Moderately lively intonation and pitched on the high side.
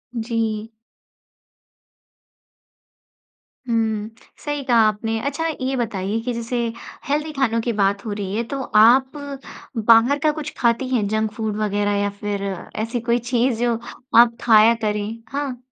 Yes: average, 3.0 semitones; high, 230 Hz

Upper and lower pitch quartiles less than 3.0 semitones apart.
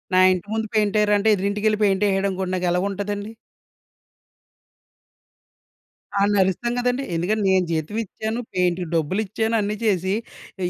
Yes: narrow, 2.5 semitones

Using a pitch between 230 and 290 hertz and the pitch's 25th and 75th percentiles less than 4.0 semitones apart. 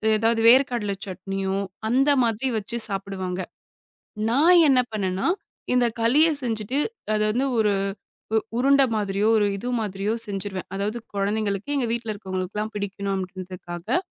No: high, 210 Hz; average, 3.5 semitones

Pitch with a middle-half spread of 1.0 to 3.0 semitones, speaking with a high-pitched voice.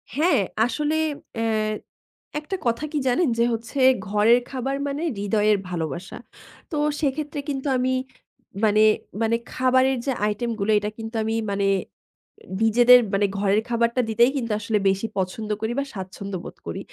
No: average, 3.9 semitones; high, 230 Hz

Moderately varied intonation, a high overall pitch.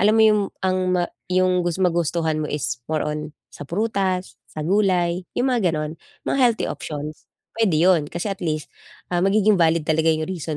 No: average, 3.6 semitones; medium, 175 Hz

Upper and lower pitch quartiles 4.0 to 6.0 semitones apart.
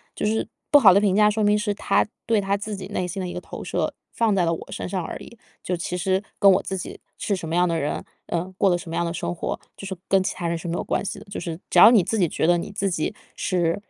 No: average, 2.7 semitones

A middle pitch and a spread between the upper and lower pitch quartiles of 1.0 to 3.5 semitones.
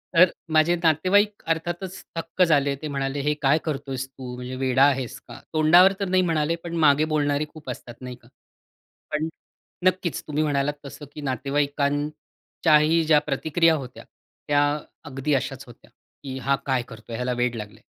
Yes: medium, 145 Hz; average, 3.0 semitones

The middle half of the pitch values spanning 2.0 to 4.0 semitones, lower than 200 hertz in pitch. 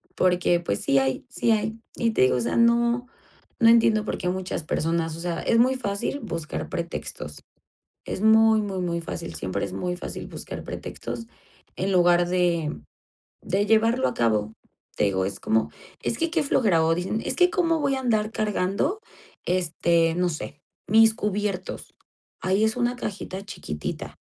No: average, 5.0 semitones; high, 190 Hz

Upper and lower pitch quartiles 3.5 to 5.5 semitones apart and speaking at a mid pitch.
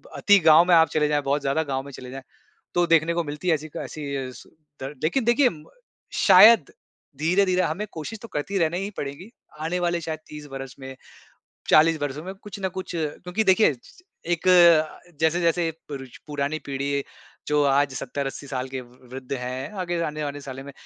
Yes: average, 4.0 semitones; medium, 150 Hz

